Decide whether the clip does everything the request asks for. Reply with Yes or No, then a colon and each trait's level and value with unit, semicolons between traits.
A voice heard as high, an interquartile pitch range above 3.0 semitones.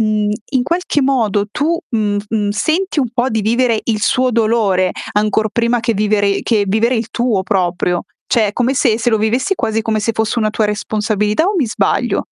No: high, 220 Hz; average, 2.7 semitones